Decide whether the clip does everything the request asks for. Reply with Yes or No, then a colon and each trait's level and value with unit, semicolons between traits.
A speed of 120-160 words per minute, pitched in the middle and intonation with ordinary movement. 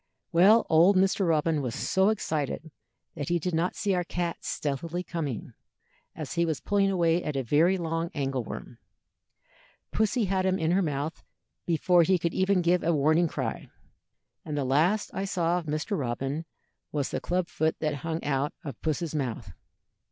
No: average, 175 wpm; medium, 165 Hz; average, 3.5 semitones